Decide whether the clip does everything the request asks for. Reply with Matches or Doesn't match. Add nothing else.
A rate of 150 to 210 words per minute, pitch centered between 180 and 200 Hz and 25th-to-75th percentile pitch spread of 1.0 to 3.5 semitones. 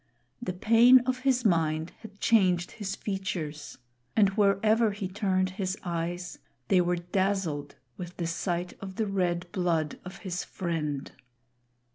Doesn't match